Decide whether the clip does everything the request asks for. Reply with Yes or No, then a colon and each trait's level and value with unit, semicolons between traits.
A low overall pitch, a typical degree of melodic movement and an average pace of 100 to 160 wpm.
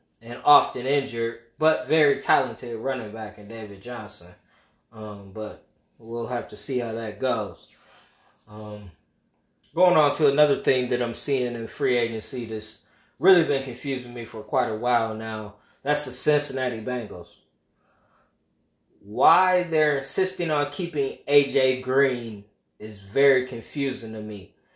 Yes: low, 120 Hz; average, 4.5 semitones; average, 140 wpm